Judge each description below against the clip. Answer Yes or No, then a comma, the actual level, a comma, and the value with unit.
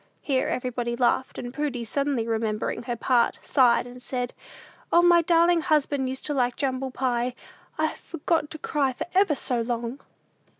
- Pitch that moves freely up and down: No, average, 3.5 semitones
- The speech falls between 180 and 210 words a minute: No, average, 165 wpm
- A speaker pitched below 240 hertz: No, very high, 260 Hz